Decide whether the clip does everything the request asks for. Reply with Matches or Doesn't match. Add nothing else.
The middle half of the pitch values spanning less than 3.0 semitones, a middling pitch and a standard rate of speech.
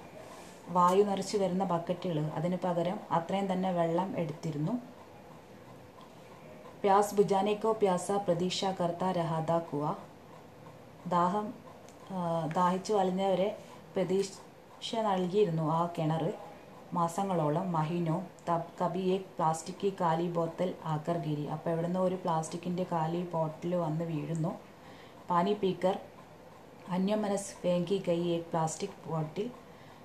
Doesn't match